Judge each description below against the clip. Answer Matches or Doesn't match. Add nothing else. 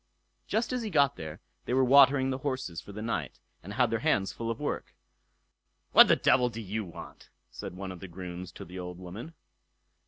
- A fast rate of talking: Matches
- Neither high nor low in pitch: Doesn't match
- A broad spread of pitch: Matches